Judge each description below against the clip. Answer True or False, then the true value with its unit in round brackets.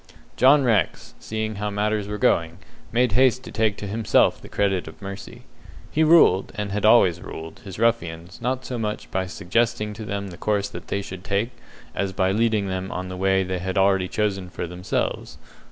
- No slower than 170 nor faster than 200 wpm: True (190 wpm)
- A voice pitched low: True (100 Hz)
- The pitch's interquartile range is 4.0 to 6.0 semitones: False (2.8 semitones)